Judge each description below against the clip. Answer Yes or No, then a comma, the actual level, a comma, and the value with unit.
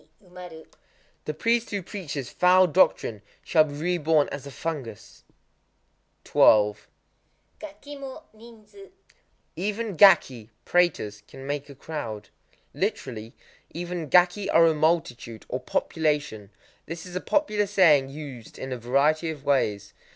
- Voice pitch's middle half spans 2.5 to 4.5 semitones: No, wide, 5.5 semitones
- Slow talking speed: Yes, slow, 125 wpm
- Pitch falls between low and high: Yes, medium, 160 Hz